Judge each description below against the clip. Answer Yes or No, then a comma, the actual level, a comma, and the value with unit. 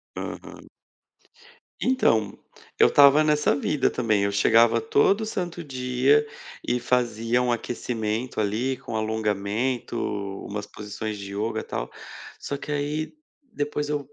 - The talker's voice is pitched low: Yes, low, 125 Hz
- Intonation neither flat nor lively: Yes, average, 4.9 semitones